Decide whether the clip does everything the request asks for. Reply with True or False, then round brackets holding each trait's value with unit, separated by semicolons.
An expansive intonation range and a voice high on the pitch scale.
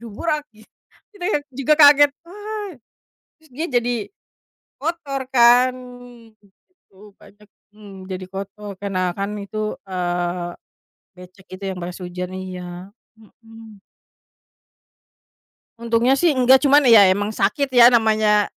True (5.8 semitones; 215 Hz)